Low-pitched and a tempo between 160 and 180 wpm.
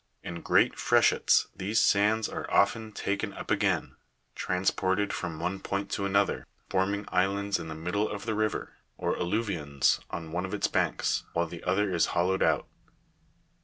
Yes: very low, 95 Hz; average, 165 wpm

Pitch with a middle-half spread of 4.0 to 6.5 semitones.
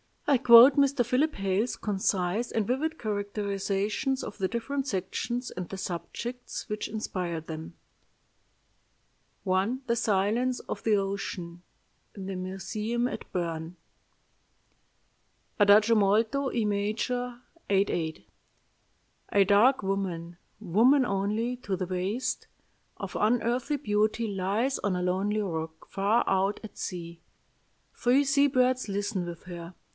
Yes: average, 4.3 semitones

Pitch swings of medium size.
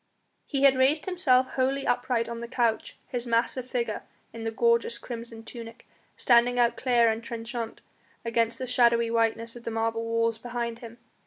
No: narrow, 1.3 semitones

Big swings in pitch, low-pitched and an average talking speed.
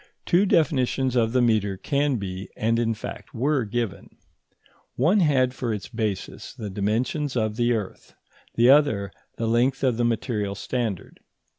No: average, 3.6 semitones; low, 120 Hz; average, 155 wpm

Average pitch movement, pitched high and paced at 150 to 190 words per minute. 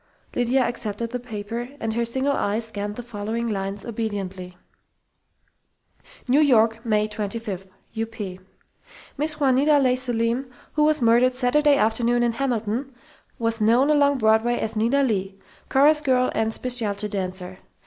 No: average, 3.2 semitones; high, 230 Hz; average, 140 wpm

